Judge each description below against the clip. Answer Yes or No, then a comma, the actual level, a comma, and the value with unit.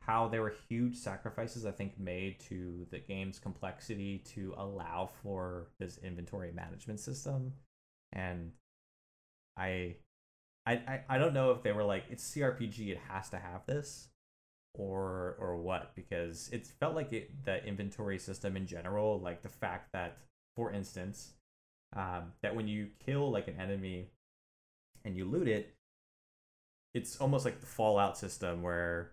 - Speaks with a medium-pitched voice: No, low, 100 Hz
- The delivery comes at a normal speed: Yes, average, 150 wpm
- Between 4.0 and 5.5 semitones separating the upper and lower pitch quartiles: Yes, average, 4.3 semitones